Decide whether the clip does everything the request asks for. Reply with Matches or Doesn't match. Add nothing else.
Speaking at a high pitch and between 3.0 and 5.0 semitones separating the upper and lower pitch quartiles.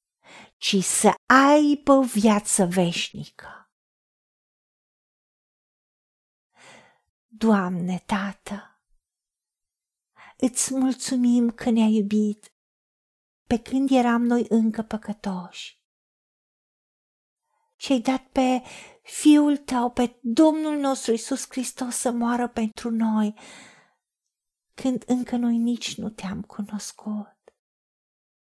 Matches